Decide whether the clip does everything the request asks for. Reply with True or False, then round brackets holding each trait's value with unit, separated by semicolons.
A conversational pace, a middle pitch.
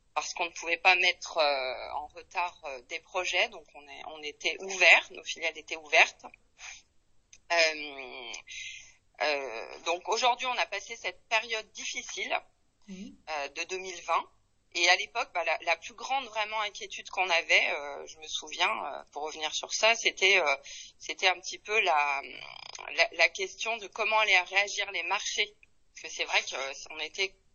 True (175 wpm; 175 Hz)